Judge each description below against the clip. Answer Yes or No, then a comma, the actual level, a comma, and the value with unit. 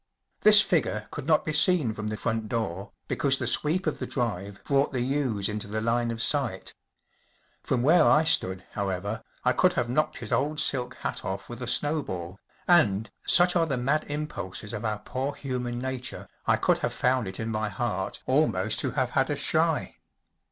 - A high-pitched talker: No, low, 125 Hz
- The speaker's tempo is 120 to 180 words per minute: No, average, 195 wpm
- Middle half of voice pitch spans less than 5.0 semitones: No, wide, 5.5 semitones